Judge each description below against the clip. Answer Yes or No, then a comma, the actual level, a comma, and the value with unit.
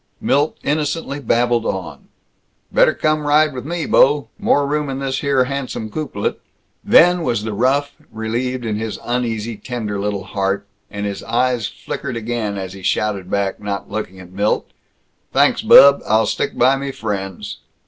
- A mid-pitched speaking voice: No, low, 120 Hz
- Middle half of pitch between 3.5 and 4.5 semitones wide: No, average, 5.1 semitones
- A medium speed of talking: Yes, average, 160 wpm